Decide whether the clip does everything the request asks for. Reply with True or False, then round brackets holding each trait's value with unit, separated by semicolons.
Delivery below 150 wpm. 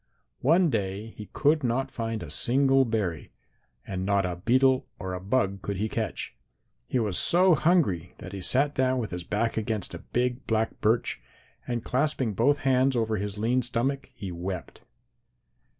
False (170 wpm)